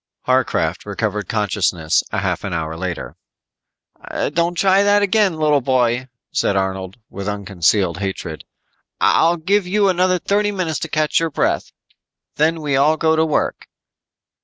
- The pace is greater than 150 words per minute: No, average, 140 wpm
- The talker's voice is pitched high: No, medium, 140 Hz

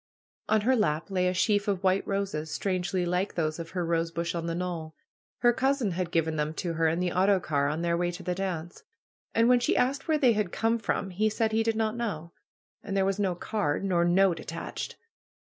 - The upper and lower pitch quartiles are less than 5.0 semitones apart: Yes, average, 4.0 semitones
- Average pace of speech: No, fast, 225 wpm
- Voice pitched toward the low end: No, medium, 185 Hz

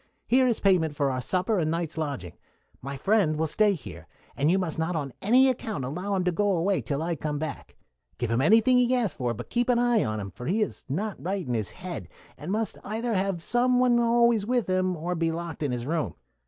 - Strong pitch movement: Yes, wide, 6.5 semitones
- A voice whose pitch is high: No, medium, 180 Hz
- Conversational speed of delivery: No, fast, 235 wpm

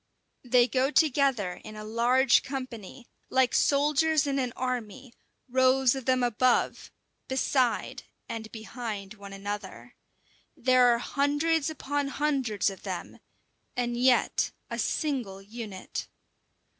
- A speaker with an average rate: No, slow, 120 wpm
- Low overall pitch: No, very high, 250 Hz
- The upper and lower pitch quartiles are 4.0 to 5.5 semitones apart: No, average, 3.5 semitones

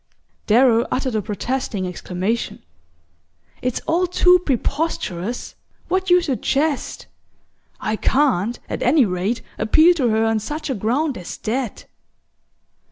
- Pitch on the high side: Yes, high, 245 Hz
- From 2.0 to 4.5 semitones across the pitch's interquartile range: No, wide, 5.6 semitones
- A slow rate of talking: Yes, slow, 120 wpm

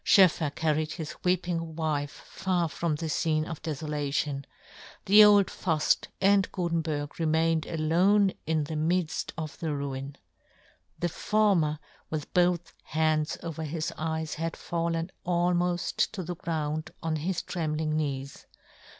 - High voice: No, medium, 160 Hz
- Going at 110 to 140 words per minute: Yes, slow, 135 wpm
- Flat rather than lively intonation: Yes, narrow, 2.2 semitones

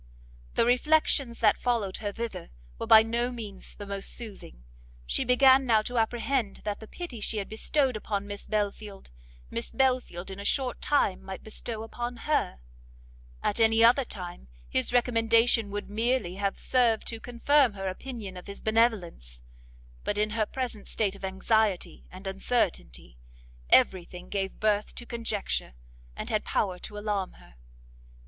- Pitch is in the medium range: No, high, 215 Hz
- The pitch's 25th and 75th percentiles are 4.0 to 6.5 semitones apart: No, average, 3.4 semitones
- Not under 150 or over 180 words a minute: Yes, average, 160 wpm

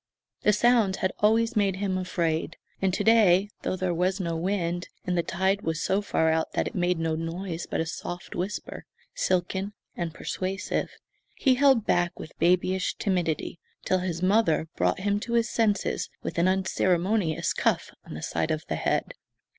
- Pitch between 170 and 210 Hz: Yes, medium, 185 Hz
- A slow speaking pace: No, average, 180 wpm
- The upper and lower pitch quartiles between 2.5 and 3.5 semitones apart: Yes, average, 2.9 semitones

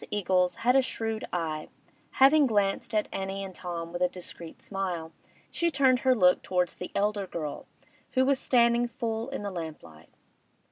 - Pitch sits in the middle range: No, high, 195 Hz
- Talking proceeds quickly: No, average, 170 wpm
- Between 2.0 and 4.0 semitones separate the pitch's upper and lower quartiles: No, average, 5.2 semitones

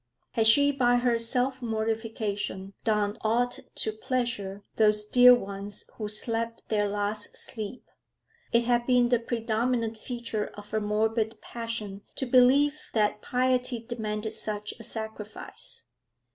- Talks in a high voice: Yes, high, 225 Hz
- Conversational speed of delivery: No, slow, 130 wpm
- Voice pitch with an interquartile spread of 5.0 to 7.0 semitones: No, narrow, 2.5 semitones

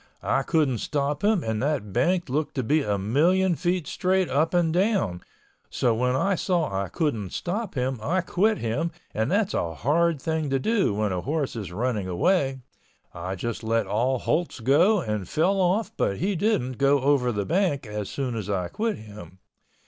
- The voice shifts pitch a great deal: Yes, wide, 8.1 semitones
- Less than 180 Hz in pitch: Yes, medium, 140 Hz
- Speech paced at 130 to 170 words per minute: No, average, 190 wpm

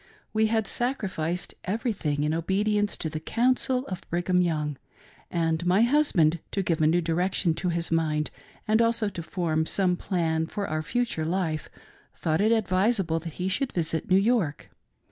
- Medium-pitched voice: Yes, medium, 180 Hz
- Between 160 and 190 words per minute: Yes, average, 165 wpm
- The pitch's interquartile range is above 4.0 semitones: Yes, average, 4.7 semitones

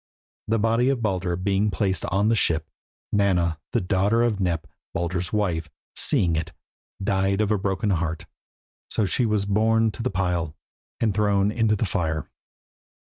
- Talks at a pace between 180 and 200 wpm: No, average, 160 wpm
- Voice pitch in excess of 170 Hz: No, low, 100 Hz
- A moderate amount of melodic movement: Yes, average, 3.3 semitones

